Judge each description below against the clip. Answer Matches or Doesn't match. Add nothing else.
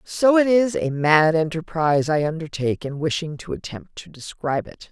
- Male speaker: Doesn't match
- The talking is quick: Doesn't match